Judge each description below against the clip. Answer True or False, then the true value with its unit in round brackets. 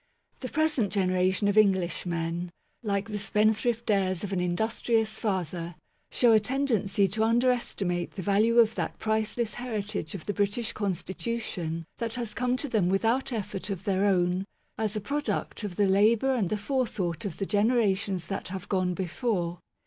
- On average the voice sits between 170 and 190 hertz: False (205 Hz)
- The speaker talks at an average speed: True (165 wpm)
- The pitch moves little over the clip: False (3.5 semitones)